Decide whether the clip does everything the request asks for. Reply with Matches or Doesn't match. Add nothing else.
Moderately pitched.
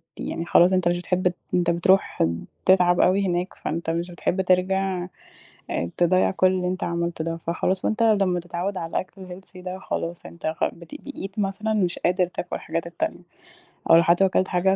Matches